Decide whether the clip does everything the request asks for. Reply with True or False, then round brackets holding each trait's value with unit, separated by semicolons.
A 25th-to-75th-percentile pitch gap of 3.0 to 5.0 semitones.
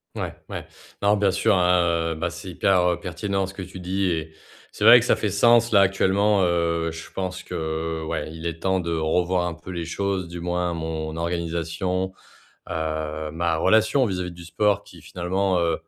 False (2.5 semitones)